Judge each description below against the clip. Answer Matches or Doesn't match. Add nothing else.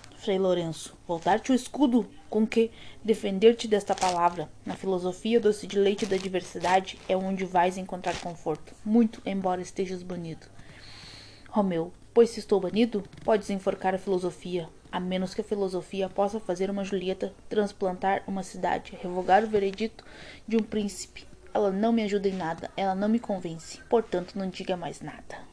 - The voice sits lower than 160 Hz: Doesn't match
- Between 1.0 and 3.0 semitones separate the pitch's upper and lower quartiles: Matches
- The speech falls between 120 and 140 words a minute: Doesn't match